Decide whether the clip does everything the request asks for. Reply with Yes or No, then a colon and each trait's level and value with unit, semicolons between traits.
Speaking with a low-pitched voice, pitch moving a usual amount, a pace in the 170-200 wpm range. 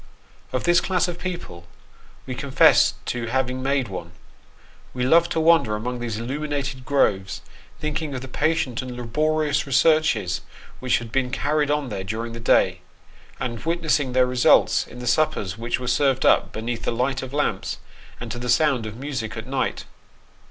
Yes: low, 130 Hz; average, 4.1 semitones; average, 175 wpm